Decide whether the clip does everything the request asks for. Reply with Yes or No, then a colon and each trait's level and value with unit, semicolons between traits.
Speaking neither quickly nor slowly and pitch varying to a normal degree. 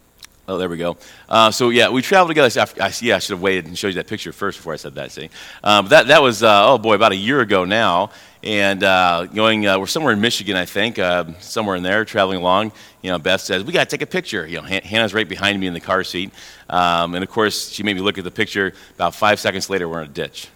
No: fast, 280 wpm; average, 3.0 semitones